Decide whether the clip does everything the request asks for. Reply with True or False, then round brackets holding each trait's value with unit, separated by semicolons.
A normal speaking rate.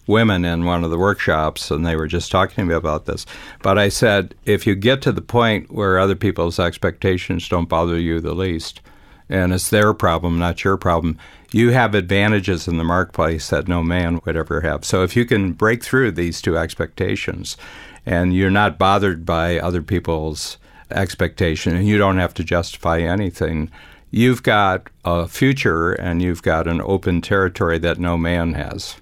True (185 wpm)